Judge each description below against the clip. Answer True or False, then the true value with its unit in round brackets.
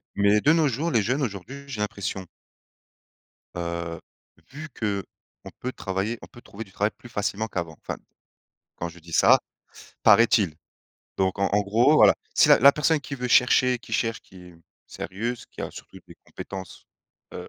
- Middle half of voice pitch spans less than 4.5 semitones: False (4.8 semitones)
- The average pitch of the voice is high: False (105 Hz)